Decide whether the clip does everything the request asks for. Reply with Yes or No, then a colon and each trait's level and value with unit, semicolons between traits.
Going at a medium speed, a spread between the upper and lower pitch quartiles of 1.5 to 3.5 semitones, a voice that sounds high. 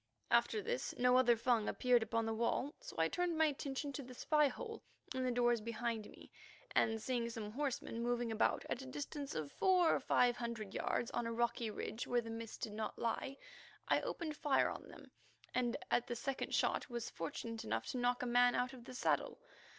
No: fast, 210 wpm; average, 2.7 semitones; high, 245 Hz